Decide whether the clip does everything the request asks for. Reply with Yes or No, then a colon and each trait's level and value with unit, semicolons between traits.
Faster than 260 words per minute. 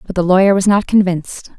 No: fast, 230 wpm